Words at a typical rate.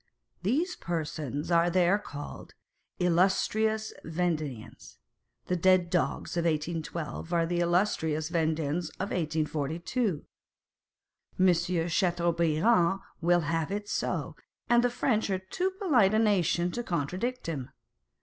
No: slow, 120 wpm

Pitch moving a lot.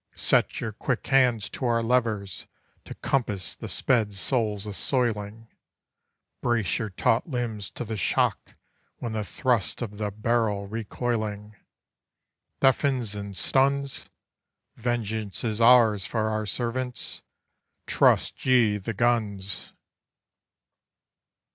No: average, 2.8 semitones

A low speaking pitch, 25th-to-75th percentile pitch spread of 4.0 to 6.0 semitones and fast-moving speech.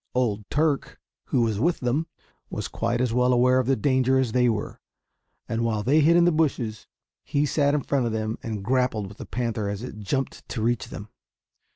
No: low, 125 Hz; average, 3.4 semitones; fast, 210 wpm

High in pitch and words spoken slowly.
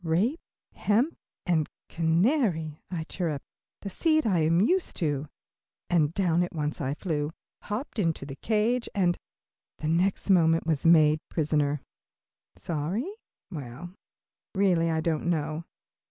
No: medium, 165 Hz; slow, 130 wpm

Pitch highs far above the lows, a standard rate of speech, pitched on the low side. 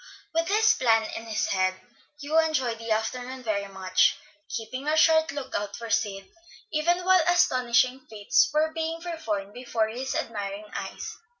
No: wide, 6.5 semitones; average, 155 wpm; very high, 250 Hz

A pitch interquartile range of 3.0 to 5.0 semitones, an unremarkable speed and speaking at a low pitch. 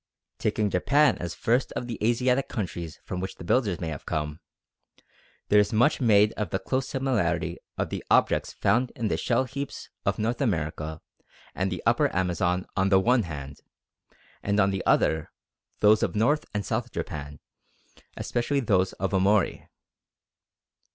No: wide, 5.4 semitones; average, 160 wpm; low, 100 Hz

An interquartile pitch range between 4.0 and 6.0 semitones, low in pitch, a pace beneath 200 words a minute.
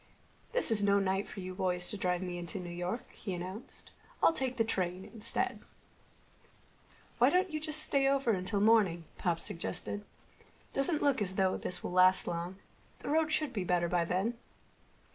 No: wide, 5.5 semitones; high, 195 Hz; average, 175 wpm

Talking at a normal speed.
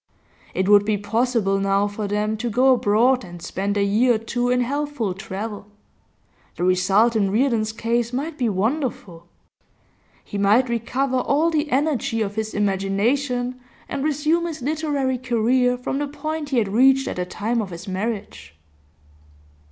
Yes: average, 160 wpm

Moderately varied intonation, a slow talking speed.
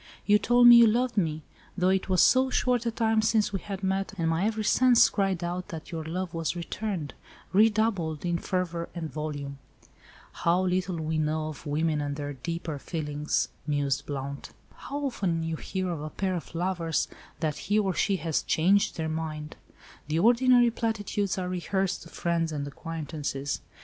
No: average, 4.6 semitones; average, 175 wpm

